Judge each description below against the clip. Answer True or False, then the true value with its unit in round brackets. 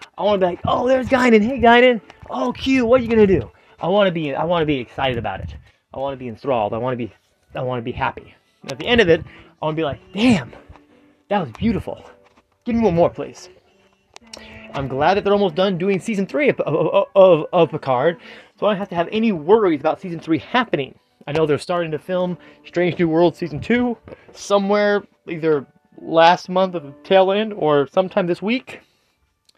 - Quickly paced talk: True (210 wpm)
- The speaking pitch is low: False (180 Hz)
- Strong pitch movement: True (5.8 semitones)